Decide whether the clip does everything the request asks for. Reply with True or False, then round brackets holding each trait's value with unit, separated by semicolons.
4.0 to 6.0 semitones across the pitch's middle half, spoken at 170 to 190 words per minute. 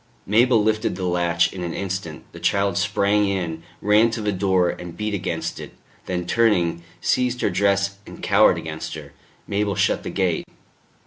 False (2.9 semitones; 175 wpm)